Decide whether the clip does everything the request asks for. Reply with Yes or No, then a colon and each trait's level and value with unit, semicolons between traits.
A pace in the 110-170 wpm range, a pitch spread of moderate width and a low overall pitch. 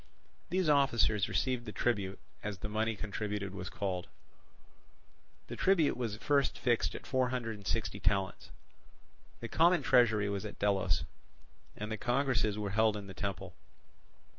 Yes: average, 150 wpm; average, 3.7 semitones; low, 110 Hz